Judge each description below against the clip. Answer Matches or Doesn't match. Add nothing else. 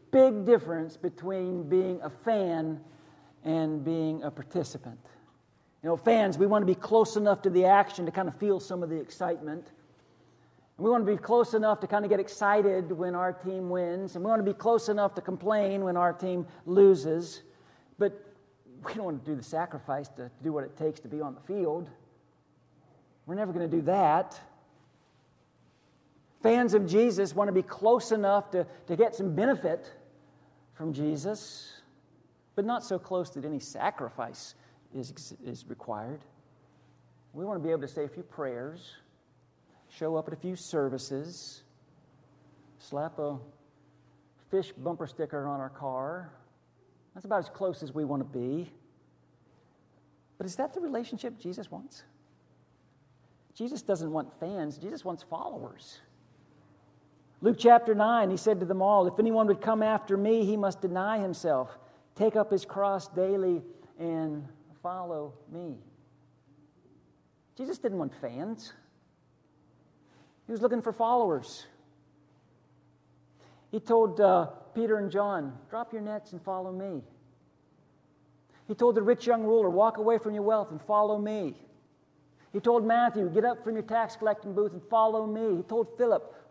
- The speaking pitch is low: Doesn't match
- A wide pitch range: Matches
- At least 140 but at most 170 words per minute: Matches